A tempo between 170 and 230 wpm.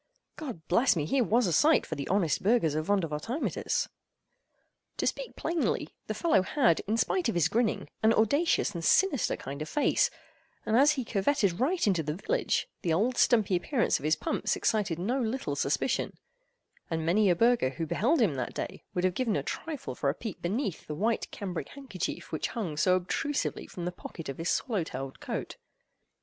Yes: average, 190 wpm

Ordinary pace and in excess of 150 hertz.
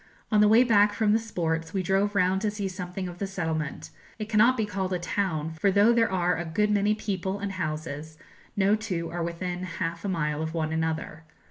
No: fast, 220 wpm; medium, 185 Hz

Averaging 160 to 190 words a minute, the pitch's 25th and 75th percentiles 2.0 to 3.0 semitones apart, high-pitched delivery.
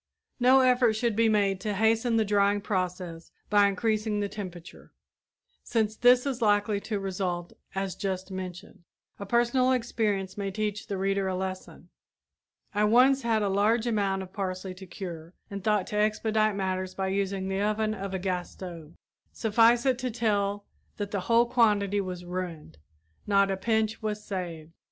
Yes: average, 170 wpm; average, 2.7 semitones; high, 200 Hz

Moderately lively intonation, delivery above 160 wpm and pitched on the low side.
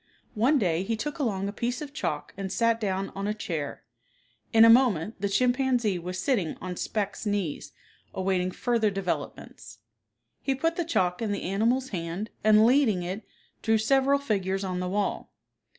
No: average, 4.5 semitones; average, 170 wpm; high, 210 Hz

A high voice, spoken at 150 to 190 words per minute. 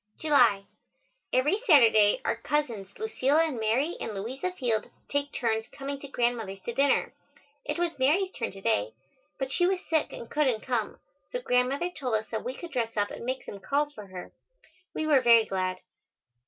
Yes: very high, 255 Hz; average, 180 wpm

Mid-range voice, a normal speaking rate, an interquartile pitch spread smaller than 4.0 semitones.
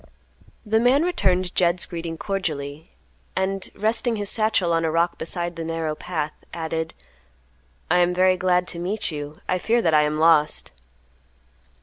Yes: medium, 175 Hz; average, 155 wpm; average, 2.8 semitones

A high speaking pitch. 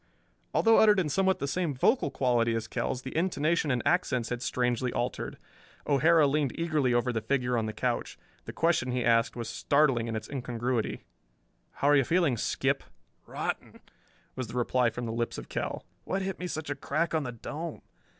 No: low, 130 Hz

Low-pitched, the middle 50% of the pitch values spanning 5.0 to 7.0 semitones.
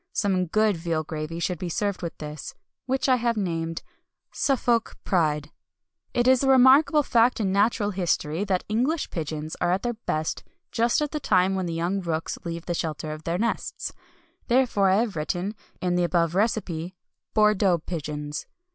No: medium, 185 Hz; wide, 5.5 semitones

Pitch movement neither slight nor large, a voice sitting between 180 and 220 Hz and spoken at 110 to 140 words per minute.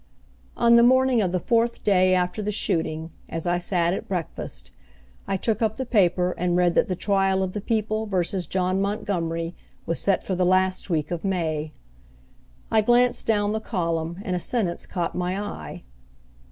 No: average, 3.5 semitones; medium, 185 Hz; average, 180 wpm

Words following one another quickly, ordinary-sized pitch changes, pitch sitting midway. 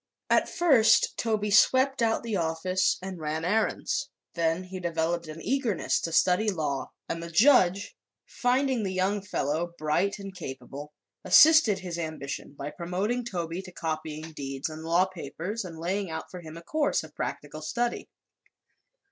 No: average, 155 wpm; average, 4.4 semitones; medium, 180 Hz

